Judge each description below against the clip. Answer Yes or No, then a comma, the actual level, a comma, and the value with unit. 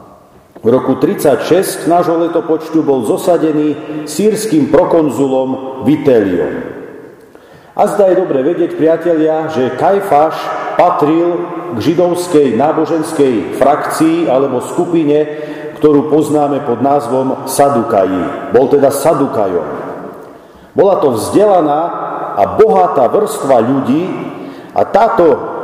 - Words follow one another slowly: Yes, slow, 100 wpm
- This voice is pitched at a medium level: Yes, medium, 155 Hz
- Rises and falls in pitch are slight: No, average, 3.3 semitones